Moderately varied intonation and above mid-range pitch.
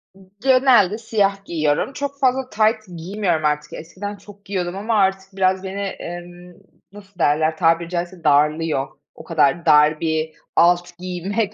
No: average, 3.8 semitones; medium, 180 Hz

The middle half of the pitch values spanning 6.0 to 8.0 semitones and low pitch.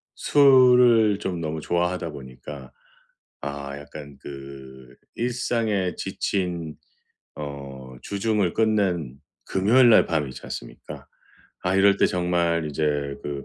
Yes: wide, 6.4 semitones; very low, 85 Hz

